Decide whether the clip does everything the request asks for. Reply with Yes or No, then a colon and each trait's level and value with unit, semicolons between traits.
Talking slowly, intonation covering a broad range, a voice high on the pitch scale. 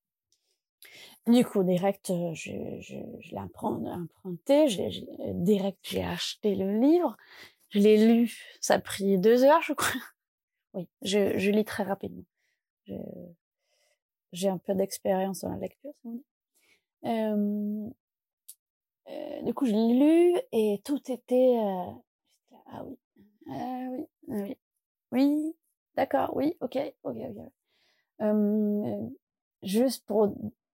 Yes: slow, 125 wpm; wide, 6.0 semitones; high, 230 Hz